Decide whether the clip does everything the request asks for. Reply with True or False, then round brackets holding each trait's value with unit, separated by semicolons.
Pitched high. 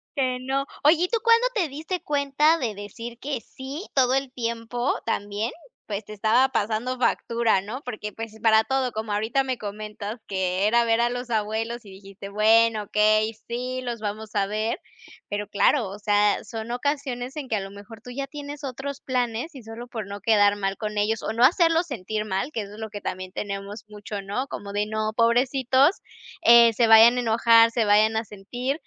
True (230 Hz)